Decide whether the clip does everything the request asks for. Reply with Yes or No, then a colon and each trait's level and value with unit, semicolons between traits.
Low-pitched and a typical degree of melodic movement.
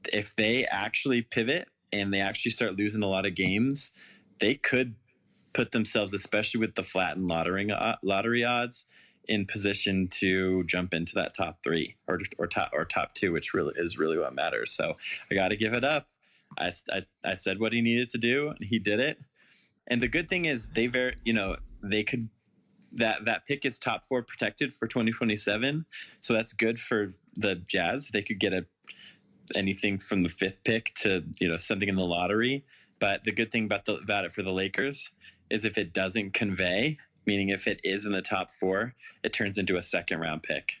Yes: low, 105 Hz; average, 3.4 semitones